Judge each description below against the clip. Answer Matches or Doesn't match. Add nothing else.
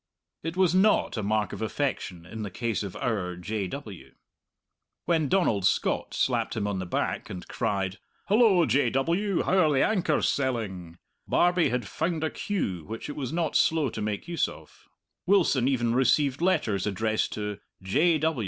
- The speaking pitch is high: Doesn't match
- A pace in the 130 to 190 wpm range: Matches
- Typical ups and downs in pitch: Doesn't match